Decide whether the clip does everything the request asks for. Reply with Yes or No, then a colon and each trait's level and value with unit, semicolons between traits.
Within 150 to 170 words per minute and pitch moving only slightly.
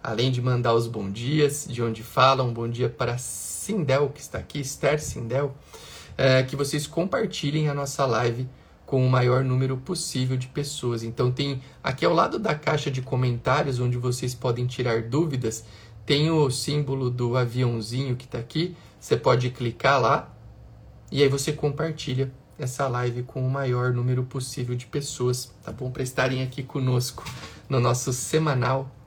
Yes: average, 165 wpm; narrow, 2.3 semitones